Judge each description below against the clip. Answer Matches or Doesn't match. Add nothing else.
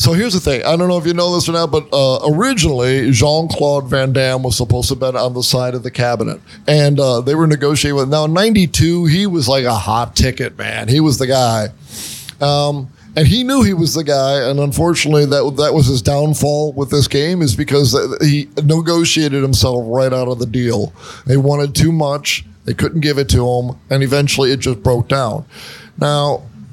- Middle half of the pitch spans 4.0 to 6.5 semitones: Doesn't match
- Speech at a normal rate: Doesn't match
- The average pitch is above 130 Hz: Matches